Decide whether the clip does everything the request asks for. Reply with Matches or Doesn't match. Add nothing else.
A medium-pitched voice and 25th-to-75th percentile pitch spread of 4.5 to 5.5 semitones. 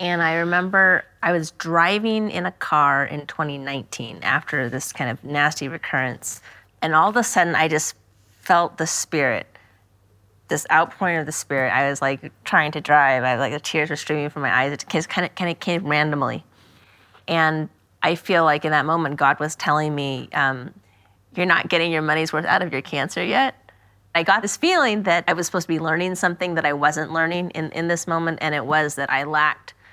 Doesn't match